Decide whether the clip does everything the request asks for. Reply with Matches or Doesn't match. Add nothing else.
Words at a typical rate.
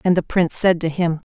Doesn't match